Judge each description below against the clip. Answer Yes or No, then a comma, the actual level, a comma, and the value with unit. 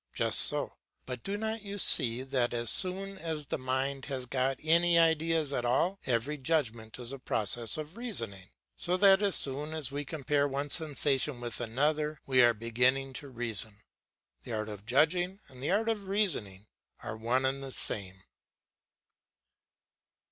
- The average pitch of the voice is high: No, low, 135 Hz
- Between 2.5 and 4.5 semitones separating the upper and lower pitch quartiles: No, average, 5.3 semitones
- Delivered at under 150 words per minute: No, average, 165 wpm